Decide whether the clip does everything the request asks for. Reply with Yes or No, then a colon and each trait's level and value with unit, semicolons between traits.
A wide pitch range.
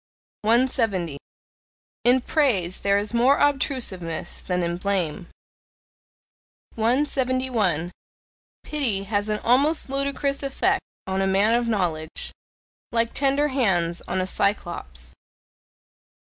Yes: wide, 6.2 semitones